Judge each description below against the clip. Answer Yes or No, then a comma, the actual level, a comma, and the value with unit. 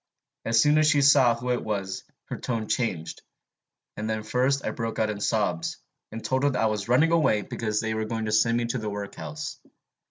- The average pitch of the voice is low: Yes, low, 115 Hz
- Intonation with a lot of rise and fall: No, average, 3.2 semitones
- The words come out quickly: Yes, fast, 215 wpm